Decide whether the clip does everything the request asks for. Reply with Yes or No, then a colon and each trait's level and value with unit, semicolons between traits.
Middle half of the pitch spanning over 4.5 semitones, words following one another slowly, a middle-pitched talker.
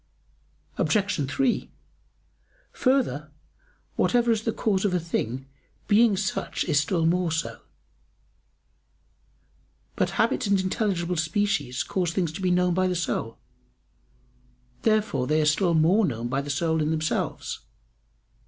Yes: average, 4.9 semitones; slow, 130 wpm; medium, 180 Hz